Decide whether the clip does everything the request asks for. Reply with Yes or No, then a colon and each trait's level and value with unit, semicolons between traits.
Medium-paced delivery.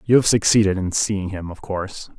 No: fast, 220 wpm